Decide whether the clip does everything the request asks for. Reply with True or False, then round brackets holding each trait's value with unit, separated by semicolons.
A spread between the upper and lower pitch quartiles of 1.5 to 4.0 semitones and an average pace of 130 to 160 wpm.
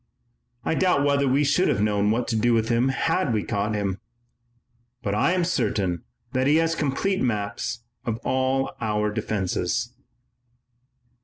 False (5.0 semitones; 155 wpm)